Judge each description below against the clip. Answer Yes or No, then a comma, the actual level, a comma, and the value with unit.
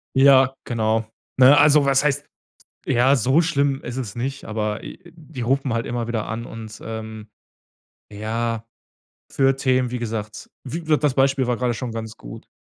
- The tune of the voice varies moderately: Yes, average, 3.3 semitones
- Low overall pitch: Yes, low, 125 Hz